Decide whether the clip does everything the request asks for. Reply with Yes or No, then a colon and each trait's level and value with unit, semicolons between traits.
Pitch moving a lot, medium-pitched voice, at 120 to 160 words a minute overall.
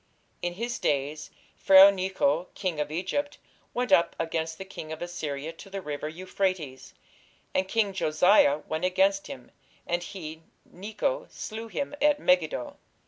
No: average, 3.9 semitones; medium, 180 Hz; average, 145 wpm